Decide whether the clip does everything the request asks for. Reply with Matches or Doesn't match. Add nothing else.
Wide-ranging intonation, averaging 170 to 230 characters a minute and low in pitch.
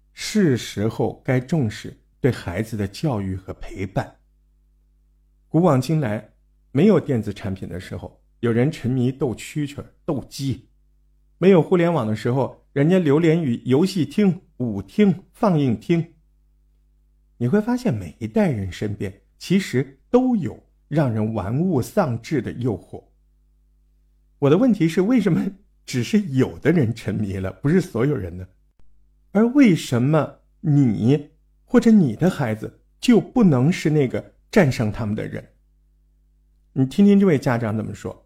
Matches